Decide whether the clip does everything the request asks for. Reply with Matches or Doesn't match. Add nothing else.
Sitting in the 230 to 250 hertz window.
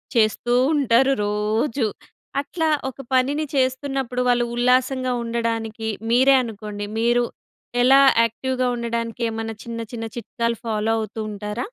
Matches